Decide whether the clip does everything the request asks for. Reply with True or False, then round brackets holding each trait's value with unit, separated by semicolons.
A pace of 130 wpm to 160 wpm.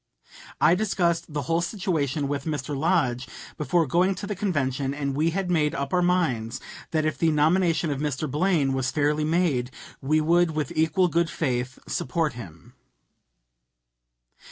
True (155 wpm)